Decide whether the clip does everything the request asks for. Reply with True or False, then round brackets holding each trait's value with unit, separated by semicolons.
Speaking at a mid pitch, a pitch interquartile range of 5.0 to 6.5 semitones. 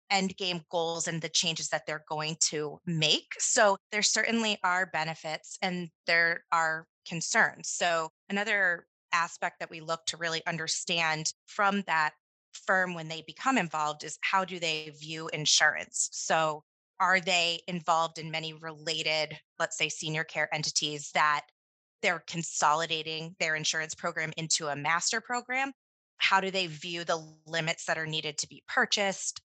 False (165 Hz; 2.6 semitones)